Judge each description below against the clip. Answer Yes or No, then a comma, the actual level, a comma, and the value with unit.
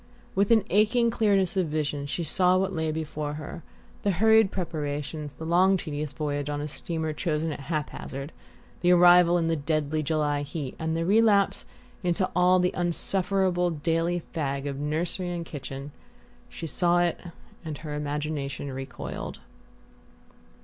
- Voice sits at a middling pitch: Yes, medium, 165 Hz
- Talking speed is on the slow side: No, average, 150 wpm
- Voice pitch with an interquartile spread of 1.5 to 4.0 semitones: Yes, average, 3.4 semitones